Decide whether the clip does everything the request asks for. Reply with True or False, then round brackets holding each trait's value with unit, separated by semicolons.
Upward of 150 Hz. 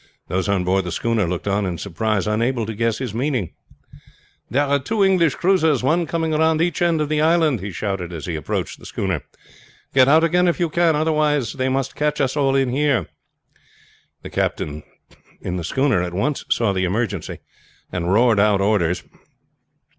False (125 Hz)